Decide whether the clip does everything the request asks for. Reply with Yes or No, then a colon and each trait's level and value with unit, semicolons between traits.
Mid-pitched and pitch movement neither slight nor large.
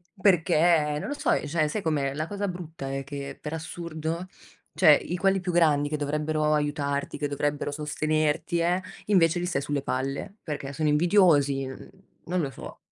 Yes: medium, 155 Hz; average, 3.1 semitones